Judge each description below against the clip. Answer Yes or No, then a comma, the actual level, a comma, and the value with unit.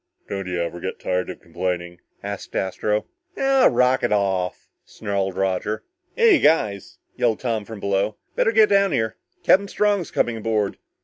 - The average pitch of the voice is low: Yes, low, 105 Hz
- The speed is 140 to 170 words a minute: Yes, average, 160 wpm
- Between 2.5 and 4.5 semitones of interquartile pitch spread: No, wide, 5.6 semitones